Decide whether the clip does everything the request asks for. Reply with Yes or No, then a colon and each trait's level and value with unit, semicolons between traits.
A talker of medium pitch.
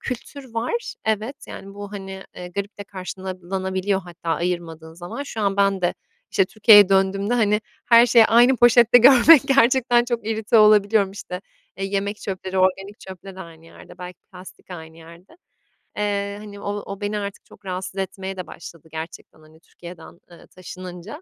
No: high, 195 Hz